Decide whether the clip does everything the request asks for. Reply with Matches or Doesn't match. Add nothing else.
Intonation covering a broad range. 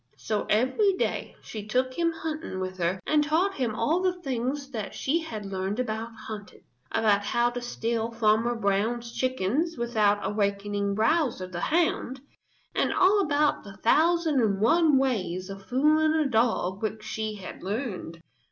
Matches